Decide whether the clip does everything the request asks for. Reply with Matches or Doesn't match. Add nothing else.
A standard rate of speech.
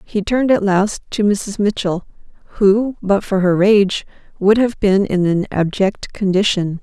Matches